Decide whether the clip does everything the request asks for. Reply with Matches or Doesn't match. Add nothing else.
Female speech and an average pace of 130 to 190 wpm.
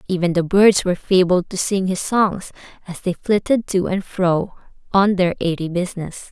Matches